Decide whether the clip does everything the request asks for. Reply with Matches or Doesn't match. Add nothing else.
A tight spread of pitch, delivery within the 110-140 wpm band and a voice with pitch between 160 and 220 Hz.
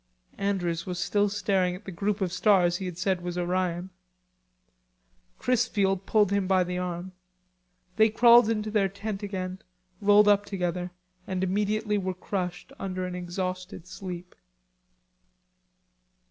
Matches